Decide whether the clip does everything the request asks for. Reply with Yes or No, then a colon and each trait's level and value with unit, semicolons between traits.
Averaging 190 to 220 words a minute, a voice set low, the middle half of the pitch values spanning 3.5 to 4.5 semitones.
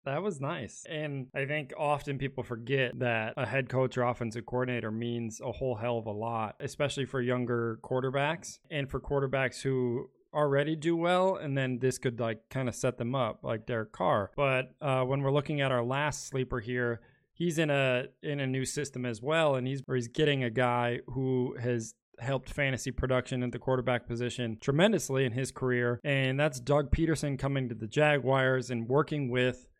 No: average, 195 wpm; low, 130 Hz; narrow, 2.4 semitones